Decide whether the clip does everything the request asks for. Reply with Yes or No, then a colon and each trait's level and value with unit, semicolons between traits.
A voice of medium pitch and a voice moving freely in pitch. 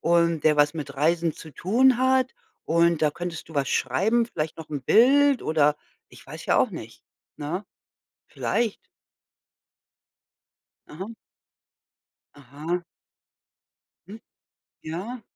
Yes: medium, 170 Hz; wide, 6.6 semitones